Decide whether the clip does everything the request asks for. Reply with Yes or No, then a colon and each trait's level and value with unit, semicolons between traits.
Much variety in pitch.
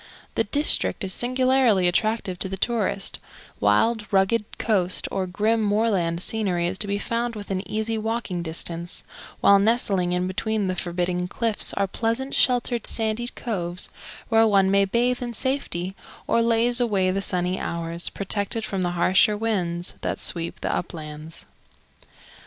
No: average, 4.1 semitones